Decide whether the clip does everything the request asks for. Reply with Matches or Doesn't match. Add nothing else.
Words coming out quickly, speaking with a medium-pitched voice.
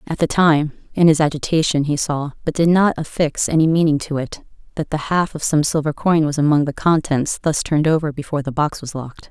Matches